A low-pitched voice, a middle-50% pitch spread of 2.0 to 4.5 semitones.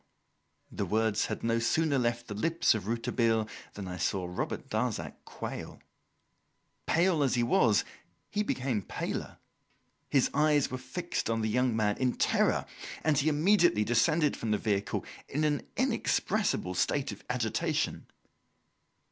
No: low, 120 Hz; average, 5.1 semitones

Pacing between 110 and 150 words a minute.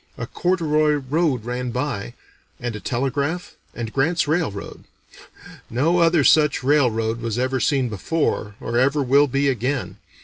Yes: average, 140 wpm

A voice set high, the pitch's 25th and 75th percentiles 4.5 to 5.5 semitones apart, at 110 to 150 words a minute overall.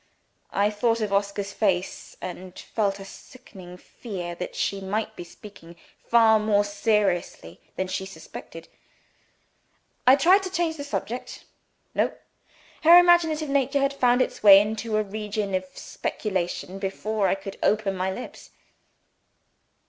No: high, 205 Hz; average, 4.0 semitones; average, 140 wpm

